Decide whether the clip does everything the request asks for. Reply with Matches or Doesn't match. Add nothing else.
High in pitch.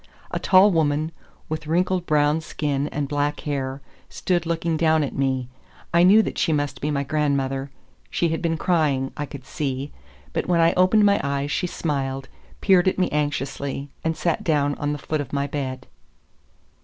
Doesn't match